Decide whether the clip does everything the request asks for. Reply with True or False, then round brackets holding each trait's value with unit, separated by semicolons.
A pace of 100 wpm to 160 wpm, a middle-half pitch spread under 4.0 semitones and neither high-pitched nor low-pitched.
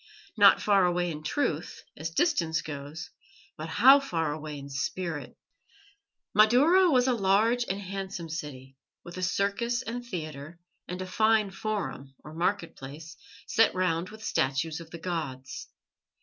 False (150 wpm; 5.5 semitones; 175 Hz)